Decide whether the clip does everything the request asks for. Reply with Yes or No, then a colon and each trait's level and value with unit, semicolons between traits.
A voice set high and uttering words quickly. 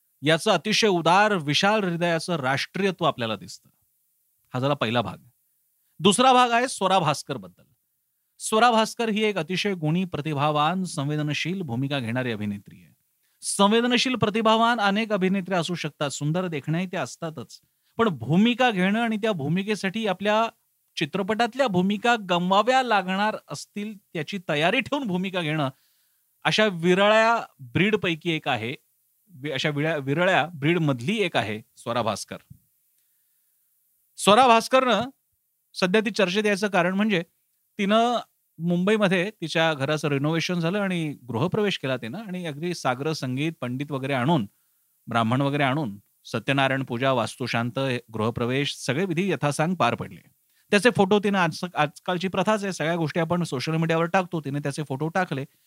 No: medium, 175 Hz; fast, 135 wpm